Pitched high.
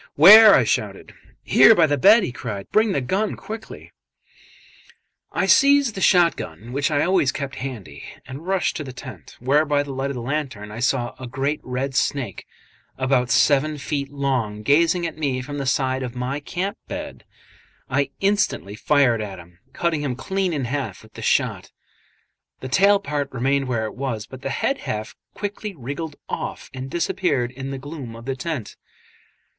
No: medium, 140 Hz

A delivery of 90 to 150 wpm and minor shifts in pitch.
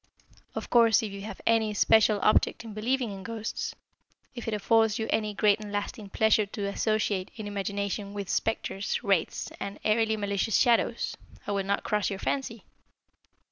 No: average, 170 wpm; narrow, 1.8 semitones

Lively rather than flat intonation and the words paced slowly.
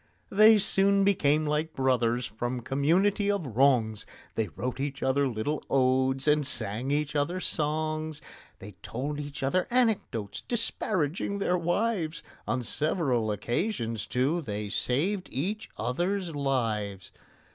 Yes: wide, 6.1 semitones; slow, 125 wpm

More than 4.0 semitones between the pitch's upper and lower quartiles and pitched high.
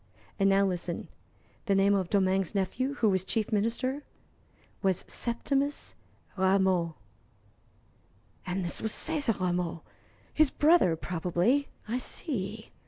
Yes: average, 4.8 semitones; high, 195 Hz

